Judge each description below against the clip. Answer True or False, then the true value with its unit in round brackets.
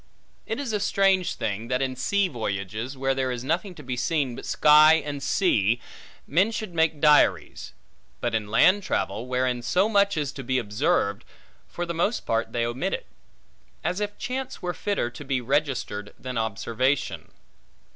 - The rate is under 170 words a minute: False (175 wpm)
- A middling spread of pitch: False (7.0 semitones)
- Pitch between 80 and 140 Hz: True (135 Hz)